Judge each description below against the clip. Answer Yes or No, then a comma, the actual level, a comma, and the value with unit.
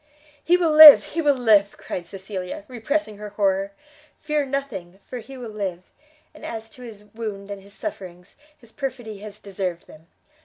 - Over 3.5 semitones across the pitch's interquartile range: Yes, average, 4.9 semitones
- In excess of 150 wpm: Yes, average, 170 wpm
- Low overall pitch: No, high, 215 Hz